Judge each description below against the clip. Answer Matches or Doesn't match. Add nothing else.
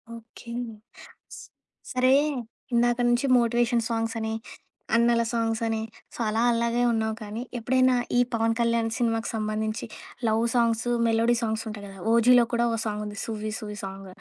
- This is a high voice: Matches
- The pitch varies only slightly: Matches